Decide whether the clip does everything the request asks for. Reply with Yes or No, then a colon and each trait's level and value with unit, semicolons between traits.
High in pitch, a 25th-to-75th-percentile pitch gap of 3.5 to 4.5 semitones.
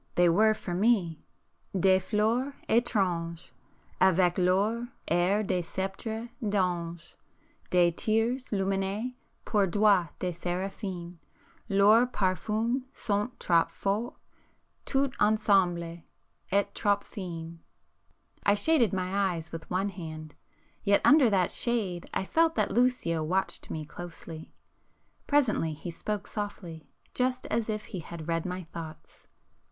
Yes: high, 195 Hz; average, 3.8 semitones